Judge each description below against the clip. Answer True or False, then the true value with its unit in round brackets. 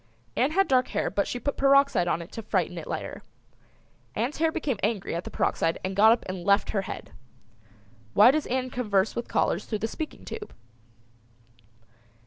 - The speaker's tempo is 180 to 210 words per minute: True (185 wpm)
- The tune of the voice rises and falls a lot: True (5.7 semitones)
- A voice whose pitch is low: False (235 Hz)